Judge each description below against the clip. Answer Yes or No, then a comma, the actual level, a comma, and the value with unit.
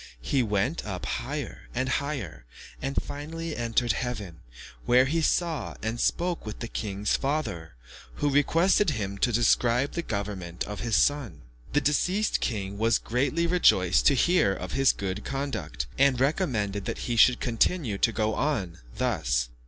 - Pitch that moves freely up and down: Yes, wide, 6.2 semitones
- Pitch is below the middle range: Yes, low, 120 Hz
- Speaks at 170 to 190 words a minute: No, average, 155 wpm